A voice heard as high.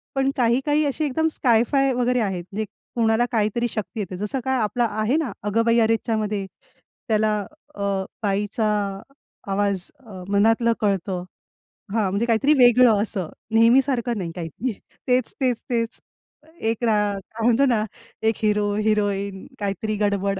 Yes: high, 220 Hz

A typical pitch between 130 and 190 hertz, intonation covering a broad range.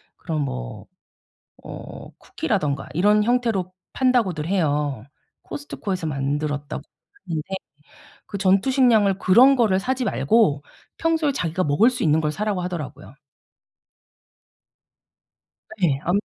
Yes: medium, 185 Hz; wide, 6.9 semitones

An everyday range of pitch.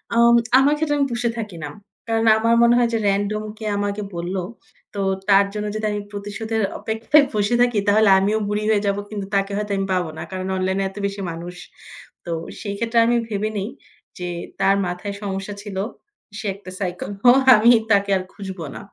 No: narrow, 2.3 semitones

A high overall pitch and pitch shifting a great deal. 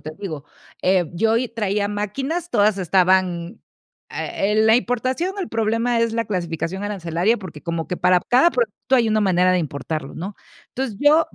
No: high, 205 Hz; average, 4.3 semitones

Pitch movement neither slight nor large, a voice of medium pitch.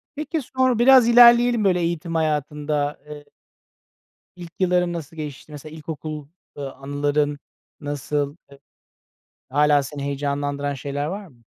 Yes: average, 3.8 semitones; medium, 150 Hz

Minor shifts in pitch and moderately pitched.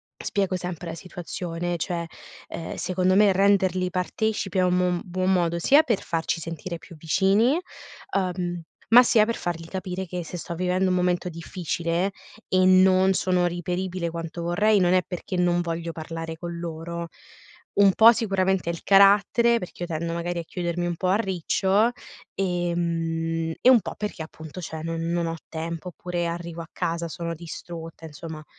Yes: narrow, 1.9 semitones; medium, 175 Hz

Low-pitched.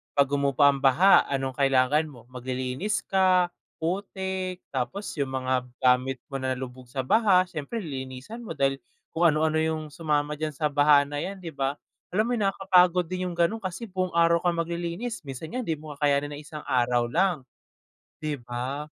No: medium, 150 Hz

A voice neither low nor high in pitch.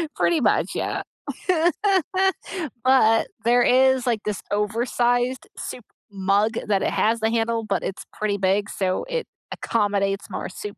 No: high, 220 Hz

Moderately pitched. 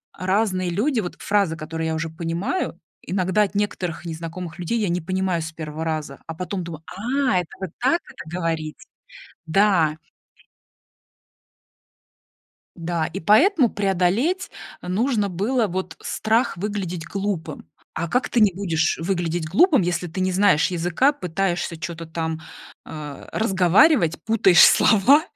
Yes: medium, 180 Hz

